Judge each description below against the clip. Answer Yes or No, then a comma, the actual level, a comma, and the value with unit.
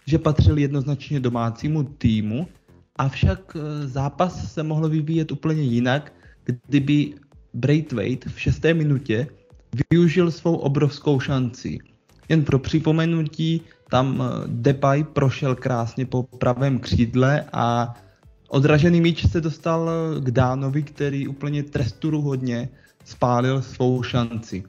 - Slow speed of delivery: Yes, slow, 105 wpm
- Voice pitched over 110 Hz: Yes, medium, 140 Hz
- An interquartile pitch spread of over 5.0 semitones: No, average, 3.6 semitones